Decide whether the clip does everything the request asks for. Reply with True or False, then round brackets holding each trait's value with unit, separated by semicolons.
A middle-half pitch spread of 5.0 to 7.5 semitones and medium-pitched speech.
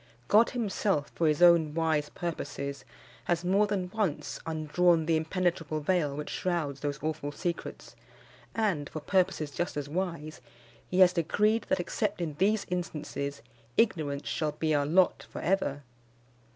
False (3.8 semitones; 165 Hz)